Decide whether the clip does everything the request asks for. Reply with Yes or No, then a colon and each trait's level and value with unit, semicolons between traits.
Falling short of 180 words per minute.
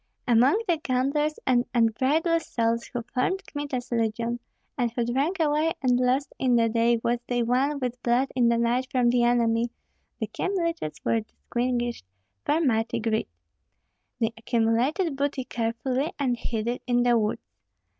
Yes: average, 155 wpm